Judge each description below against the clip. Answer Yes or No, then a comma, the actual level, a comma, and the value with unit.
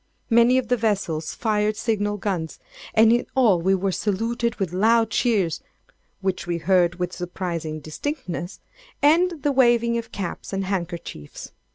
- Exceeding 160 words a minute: No, average, 150 wpm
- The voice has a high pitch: Yes, high, 205 Hz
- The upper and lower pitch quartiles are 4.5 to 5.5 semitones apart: Yes, average, 4.8 semitones